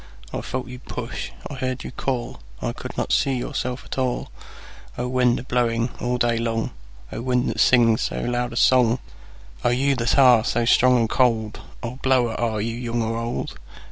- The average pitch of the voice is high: No, low, 120 Hz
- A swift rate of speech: No, average, 170 wpm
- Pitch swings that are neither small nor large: No, narrow, 1.6 semitones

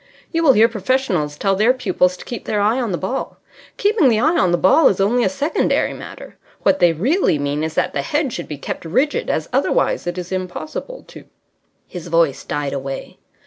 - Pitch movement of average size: No, wide, 7.6 semitones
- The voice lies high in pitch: Yes, high, 195 Hz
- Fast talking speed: Yes, fast, 215 wpm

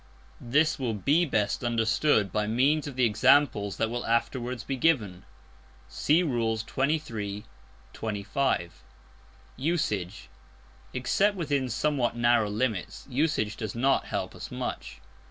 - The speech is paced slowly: Yes, slow, 120 wpm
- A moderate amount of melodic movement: Yes, average, 4.9 semitones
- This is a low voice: Yes, low, 120 Hz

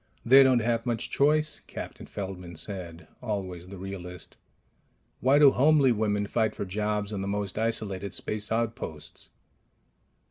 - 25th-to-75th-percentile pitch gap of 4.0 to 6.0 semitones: No, average, 3.6 semitones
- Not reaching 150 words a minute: Yes, average, 140 wpm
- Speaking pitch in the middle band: No, low, 105 Hz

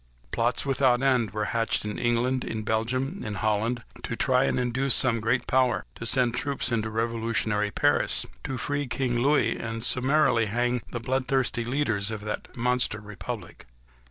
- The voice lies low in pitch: Yes, low, 120 Hz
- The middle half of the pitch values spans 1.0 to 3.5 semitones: Yes, narrow, 2.5 semitones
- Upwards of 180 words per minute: No, average, 165 wpm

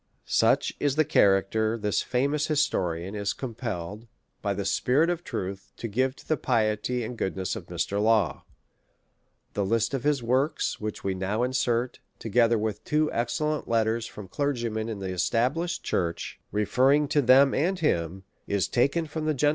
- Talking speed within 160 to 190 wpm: Yes, average, 170 wpm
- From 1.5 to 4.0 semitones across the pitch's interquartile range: No, wide, 5.4 semitones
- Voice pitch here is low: Yes, low, 115 Hz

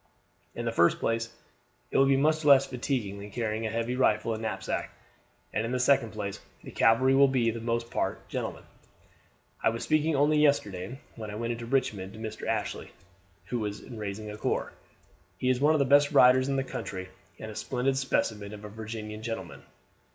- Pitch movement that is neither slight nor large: Yes, average, 3.7 semitones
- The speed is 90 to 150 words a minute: No, average, 200 wpm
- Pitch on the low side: Yes, low, 115 Hz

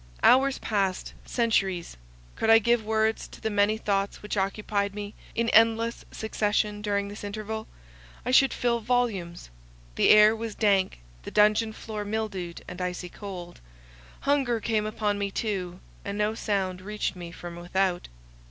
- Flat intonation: Yes, narrow, 2.3 semitones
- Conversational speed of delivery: Yes, average, 150 wpm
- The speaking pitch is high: Yes, high, 210 Hz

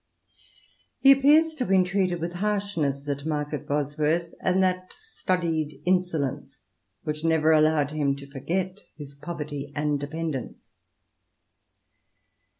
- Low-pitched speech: No, medium, 160 Hz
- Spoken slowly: Yes, slow, 120 wpm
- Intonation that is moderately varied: Yes, average, 4.0 semitones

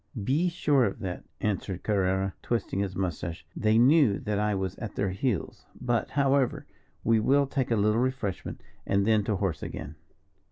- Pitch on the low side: Yes, low, 105 Hz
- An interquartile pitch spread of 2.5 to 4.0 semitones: No, average, 4.7 semitones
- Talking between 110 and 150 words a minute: No, average, 170 wpm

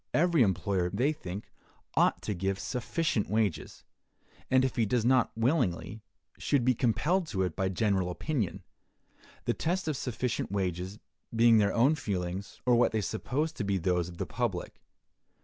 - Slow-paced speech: No, average, 165 wpm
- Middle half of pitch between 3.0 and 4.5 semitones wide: No, average, 5.3 semitones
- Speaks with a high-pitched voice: No, low, 110 Hz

